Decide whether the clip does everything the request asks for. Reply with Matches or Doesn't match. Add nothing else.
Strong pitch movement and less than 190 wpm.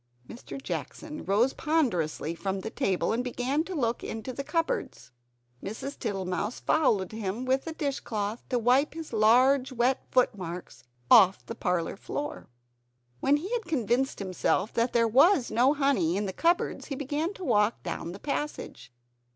Matches